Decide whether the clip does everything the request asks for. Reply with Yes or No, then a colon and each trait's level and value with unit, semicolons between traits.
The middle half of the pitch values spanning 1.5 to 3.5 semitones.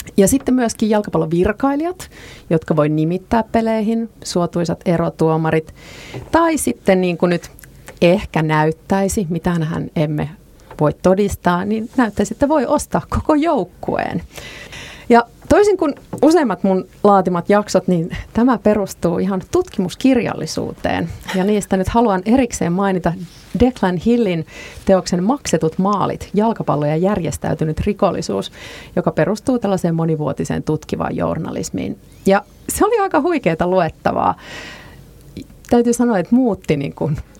No: wide, 5.4 semitones